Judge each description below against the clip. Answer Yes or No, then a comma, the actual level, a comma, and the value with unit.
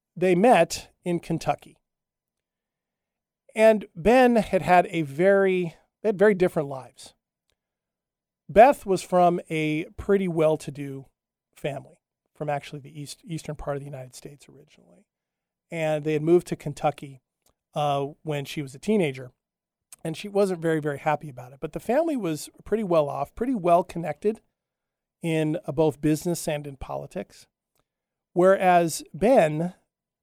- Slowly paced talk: No, average, 145 wpm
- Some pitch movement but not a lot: Yes, average, 3.8 semitones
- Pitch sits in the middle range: Yes, medium, 160 Hz